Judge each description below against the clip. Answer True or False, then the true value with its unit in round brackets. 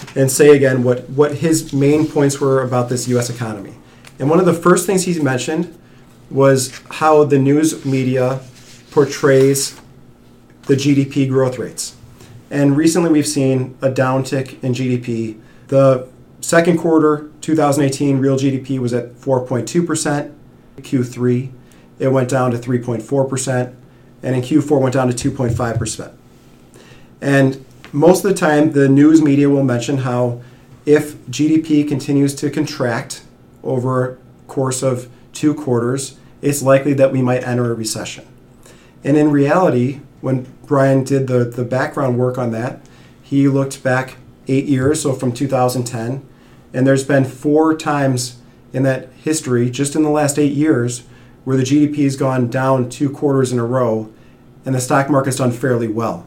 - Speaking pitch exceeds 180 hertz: False (135 Hz)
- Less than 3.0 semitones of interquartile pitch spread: True (2.5 semitones)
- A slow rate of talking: False (155 wpm)